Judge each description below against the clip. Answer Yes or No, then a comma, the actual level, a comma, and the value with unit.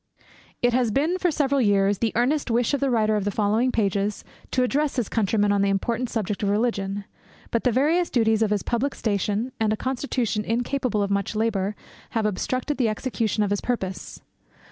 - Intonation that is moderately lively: Yes, average, 3.7 semitones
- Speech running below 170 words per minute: No, average, 195 wpm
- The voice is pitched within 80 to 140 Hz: No, high, 225 Hz